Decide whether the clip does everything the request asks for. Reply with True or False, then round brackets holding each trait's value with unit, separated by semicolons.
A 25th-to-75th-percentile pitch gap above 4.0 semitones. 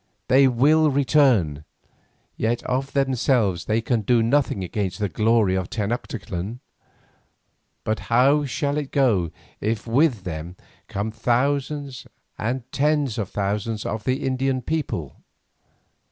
True (4.6 semitones)